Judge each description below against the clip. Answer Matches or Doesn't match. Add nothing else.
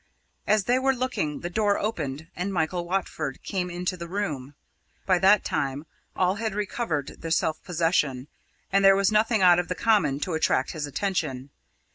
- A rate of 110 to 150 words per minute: Doesn't match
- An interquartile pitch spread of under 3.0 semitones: Doesn't match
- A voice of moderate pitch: Matches